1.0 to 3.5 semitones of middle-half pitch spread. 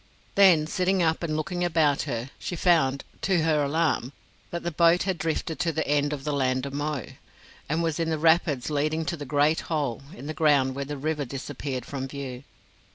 Yes: average, 2.9 semitones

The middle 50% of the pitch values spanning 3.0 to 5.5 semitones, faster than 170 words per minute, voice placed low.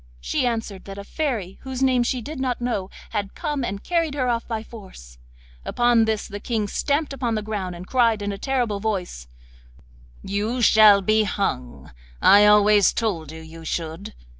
No: average, 3.7 semitones; average, 180 wpm; high, 215 Hz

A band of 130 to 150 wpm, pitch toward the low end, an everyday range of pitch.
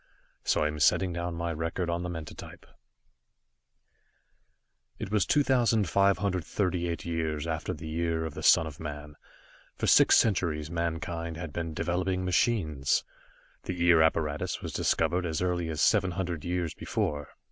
No: average, 145 wpm; very low, 85 Hz; narrow, 2.3 semitones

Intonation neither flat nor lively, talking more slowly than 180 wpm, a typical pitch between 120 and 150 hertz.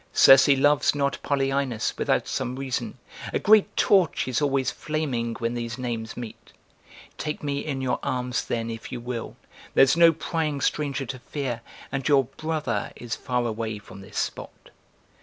Yes: average, 3.4 semitones; average, 160 wpm; low, 135 Hz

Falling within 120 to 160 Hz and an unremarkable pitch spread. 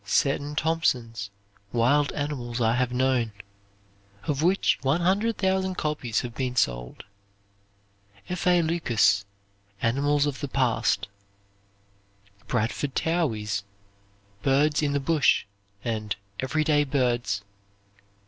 Yes: low, 135 Hz; average, 4.6 semitones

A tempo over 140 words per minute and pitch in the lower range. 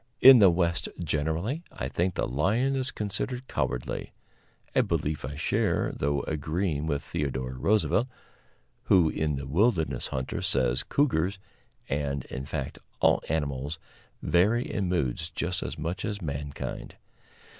No: slow, 135 wpm; very low, 80 Hz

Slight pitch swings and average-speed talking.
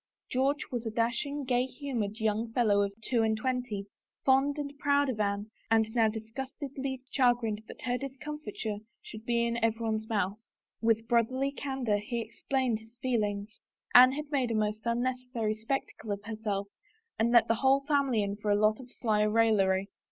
No: average, 3.3 semitones; average, 175 wpm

